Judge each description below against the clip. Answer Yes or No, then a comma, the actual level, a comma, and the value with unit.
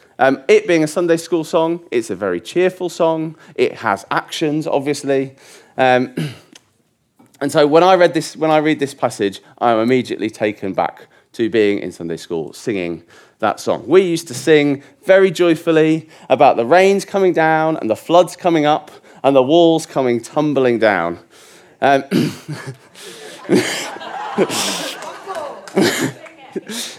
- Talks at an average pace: Yes, average, 145 wpm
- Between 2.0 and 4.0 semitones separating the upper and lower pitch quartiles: No, average, 4.5 semitones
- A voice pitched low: No, medium, 155 Hz